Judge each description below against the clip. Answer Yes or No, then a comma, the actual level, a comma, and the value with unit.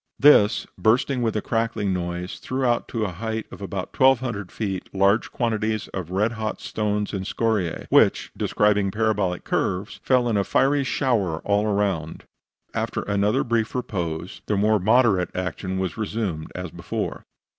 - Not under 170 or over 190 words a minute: No, average, 155 wpm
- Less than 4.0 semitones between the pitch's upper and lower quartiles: Yes, average, 3.2 semitones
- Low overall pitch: Yes, low, 105 Hz